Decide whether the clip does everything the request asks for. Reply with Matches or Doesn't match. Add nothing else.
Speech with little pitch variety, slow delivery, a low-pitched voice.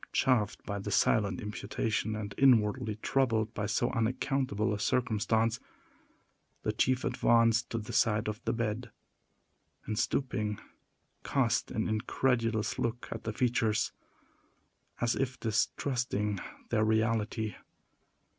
Matches